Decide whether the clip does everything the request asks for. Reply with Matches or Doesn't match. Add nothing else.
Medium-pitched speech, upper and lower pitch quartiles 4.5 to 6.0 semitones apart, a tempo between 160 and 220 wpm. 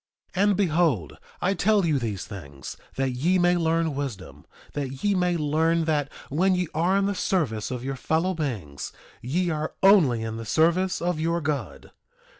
Matches